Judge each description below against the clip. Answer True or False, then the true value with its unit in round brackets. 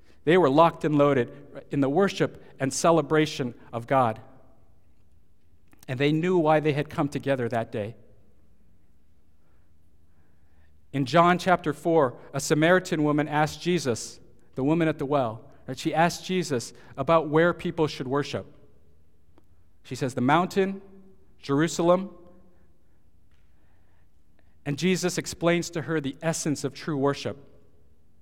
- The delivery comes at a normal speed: False (130 wpm)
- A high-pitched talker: False (135 Hz)